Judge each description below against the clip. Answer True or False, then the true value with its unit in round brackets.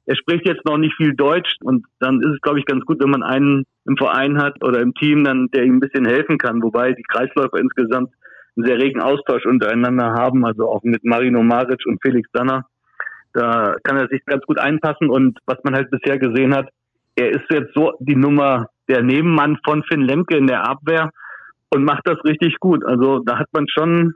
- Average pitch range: True (3.0 semitones)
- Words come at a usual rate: False (215 wpm)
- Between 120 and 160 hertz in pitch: True (135 Hz)